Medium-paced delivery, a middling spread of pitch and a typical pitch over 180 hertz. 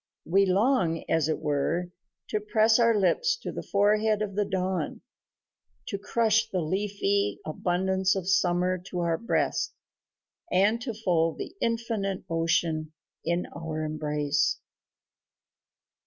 No: slow, 125 wpm; average, 4.4 semitones; high, 190 Hz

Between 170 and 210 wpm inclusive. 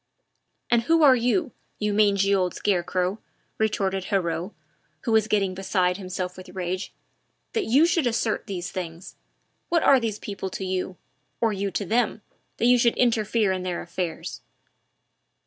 No: average, 155 wpm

